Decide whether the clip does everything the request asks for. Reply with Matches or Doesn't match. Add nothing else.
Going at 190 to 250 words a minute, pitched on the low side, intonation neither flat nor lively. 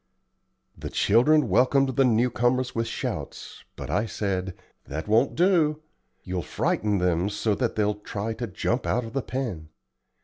Doesn't match